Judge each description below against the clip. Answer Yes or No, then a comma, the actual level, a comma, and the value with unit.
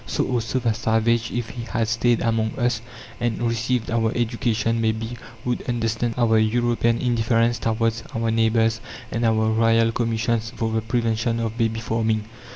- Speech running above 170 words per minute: No, average, 160 wpm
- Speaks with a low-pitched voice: Yes, low, 115 Hz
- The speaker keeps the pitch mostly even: Yes, narrow, 0.9 semitones